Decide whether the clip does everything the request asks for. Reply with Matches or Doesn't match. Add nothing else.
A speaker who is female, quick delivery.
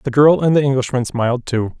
Doesn't match